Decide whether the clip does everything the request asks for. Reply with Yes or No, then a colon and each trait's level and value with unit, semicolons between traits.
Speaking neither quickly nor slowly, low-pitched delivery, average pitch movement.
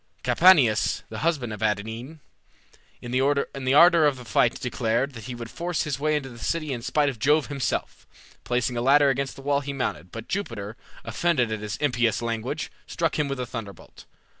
Yes: average, 190 wpm; low, 130 Hz; average, 4.1 semitones